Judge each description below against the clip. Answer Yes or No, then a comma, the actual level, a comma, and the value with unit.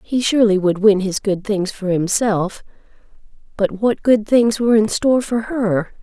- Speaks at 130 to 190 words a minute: Yes, average, 180 wpm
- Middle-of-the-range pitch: No, high, 210 Hz